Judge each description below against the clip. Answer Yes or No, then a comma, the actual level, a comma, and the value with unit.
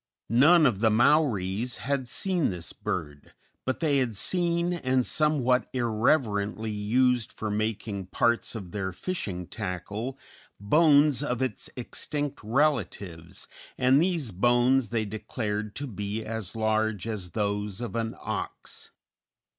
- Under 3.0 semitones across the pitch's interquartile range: No, average, 4.6 semitones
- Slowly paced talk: Yes, slow, 130 wpm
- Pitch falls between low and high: No, low, 115 Hz